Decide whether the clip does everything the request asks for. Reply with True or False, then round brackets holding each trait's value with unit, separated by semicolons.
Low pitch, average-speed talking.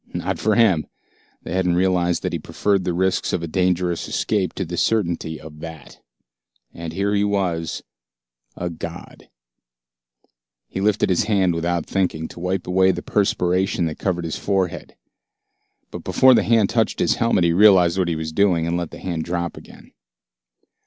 True (90 Hz; 175 wpm)